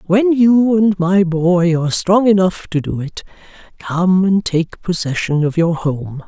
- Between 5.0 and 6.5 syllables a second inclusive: No, 3.9 syllables/s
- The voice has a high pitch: No, medium, 180 Hz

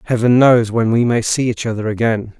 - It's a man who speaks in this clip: Yes, male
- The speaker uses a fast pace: Yes, fast, 225 wpm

